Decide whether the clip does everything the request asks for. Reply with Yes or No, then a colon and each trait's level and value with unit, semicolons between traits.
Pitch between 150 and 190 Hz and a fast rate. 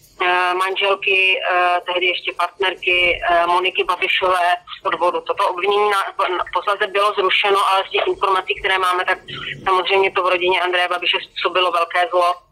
No: medium, 185 Hz; average, 145 wpm